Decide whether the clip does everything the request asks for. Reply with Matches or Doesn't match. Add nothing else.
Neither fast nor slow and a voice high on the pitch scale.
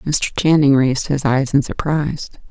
Doesn't match